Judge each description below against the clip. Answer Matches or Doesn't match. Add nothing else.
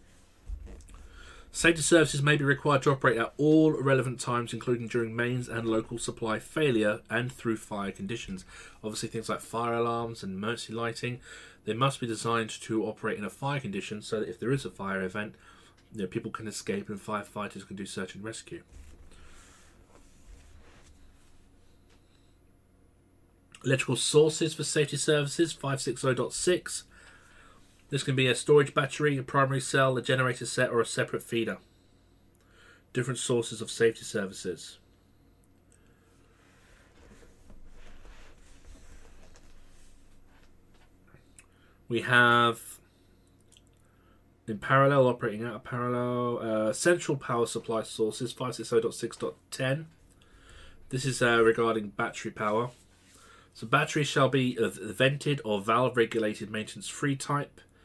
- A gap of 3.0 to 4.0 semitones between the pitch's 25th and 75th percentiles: Doesn't match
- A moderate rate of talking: Doesn't match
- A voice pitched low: Matches